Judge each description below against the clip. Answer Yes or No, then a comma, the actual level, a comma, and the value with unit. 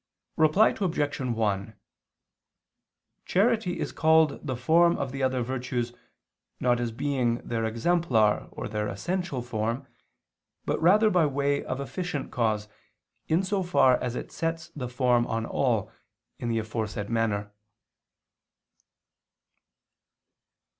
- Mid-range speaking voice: No, low, 130 Hz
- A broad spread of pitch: Yes, wide, 5.9 semitones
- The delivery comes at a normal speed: No, slow, 120 wpm